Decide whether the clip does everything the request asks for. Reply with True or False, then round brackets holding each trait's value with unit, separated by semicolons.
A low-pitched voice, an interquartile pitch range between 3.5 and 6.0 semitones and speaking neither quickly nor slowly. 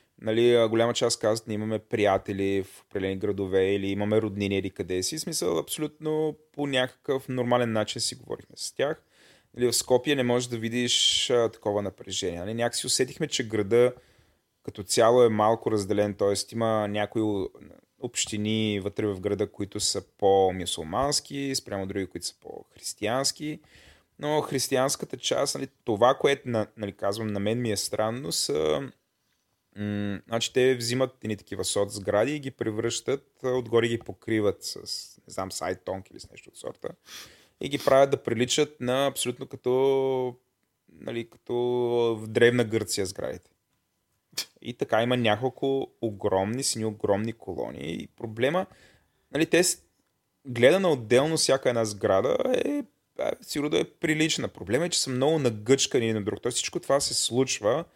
True (115 Hz; 4.0 semitones; 155 wpm)